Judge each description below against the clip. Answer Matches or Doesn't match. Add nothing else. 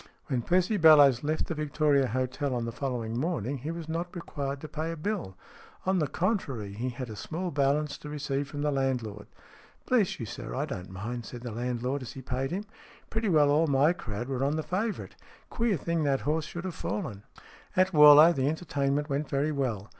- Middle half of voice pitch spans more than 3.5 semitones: Matches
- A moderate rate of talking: Doesn't match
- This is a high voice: Doesn't match